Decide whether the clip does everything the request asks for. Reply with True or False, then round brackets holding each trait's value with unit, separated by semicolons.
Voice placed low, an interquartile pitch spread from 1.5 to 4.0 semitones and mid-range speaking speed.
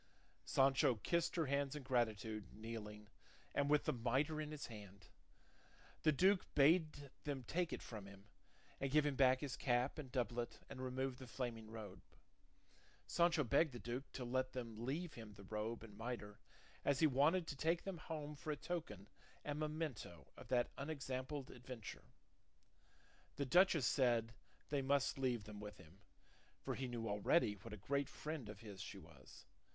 False (130 Hz; 4.8 semitones; 170 wpm)